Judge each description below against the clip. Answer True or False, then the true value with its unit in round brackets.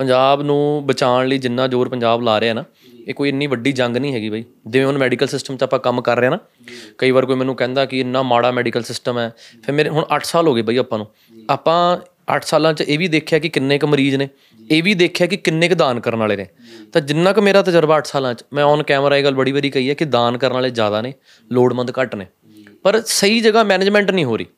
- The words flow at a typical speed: False (255 wpm)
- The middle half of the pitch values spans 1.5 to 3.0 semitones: False (3.7 semitones)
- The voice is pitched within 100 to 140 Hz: True (135 Hz)